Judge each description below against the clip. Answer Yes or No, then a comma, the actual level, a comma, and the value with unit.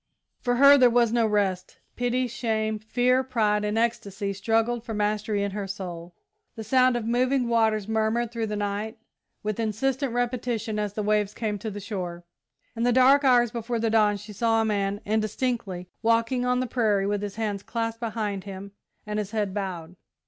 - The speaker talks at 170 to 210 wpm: Yes, average, 185 wpm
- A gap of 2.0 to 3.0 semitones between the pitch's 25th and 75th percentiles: Yes, narrow, 2.6 semitones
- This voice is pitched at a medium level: No, high, 220 Hz